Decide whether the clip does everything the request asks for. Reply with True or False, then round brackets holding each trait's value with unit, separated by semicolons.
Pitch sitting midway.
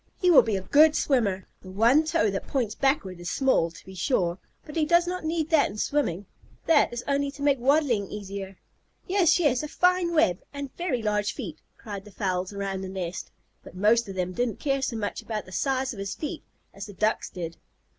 False (225 Hz)